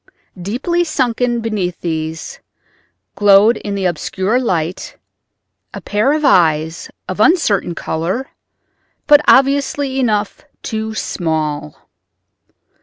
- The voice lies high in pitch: Yes, high, 205 Hz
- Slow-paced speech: Yes, slow, 100 wpm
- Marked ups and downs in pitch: Yes, wide, 6.8 semitones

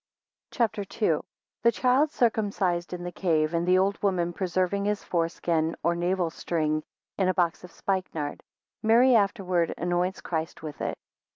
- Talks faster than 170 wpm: No, average, 165 wpm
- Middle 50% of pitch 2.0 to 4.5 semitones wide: Yes, average, 3.0 semitones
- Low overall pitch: No, medium, 180 Hz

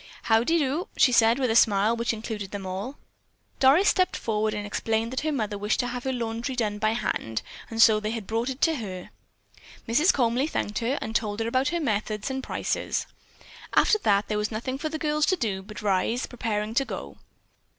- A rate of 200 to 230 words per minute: Yes, fast, 205 wpm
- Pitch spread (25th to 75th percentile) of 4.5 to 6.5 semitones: No, average, 3.8 semitones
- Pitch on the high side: Yes, high, 230 Hz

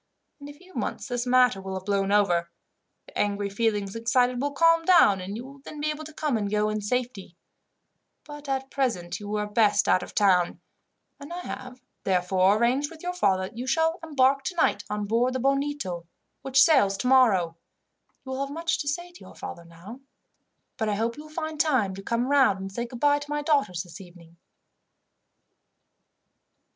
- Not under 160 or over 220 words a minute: Yes, average, 195 wpm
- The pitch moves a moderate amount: No, wide, 6.3 semitones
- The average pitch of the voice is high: Yes, high, 245 Hz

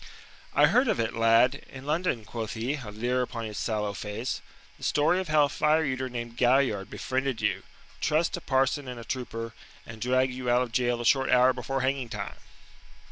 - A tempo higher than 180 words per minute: Yes, average, 200 wpm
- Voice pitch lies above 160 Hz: No, low, 125 Hz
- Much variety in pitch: No, average, 2.8 semitones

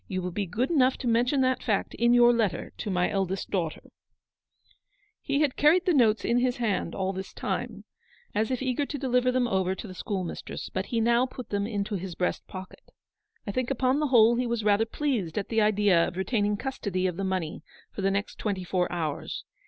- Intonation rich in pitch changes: No, average, 4.8 semitones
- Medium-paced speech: No, fast, 215 wpm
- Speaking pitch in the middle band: No, high, 215 Hz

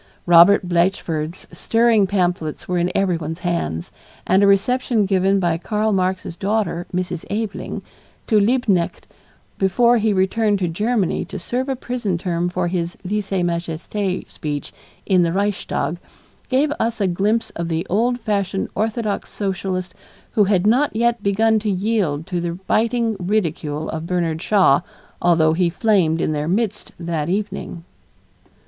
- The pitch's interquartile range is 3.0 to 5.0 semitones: Yes, average, 3.7 semitones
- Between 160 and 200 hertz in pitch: Yes, high, 190 Hz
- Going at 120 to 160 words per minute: Yes, average, 145 wpm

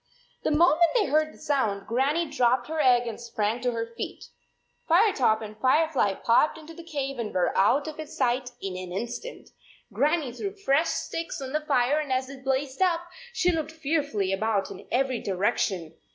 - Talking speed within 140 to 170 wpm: No, average, 190 wpm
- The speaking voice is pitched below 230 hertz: No, very high, 265 Hz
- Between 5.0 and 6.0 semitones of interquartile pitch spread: Yes, average, 5.3 semitones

